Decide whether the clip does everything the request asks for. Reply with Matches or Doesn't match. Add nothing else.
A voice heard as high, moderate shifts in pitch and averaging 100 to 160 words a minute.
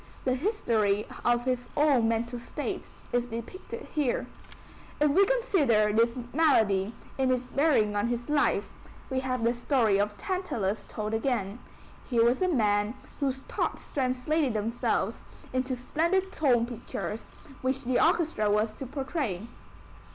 Matches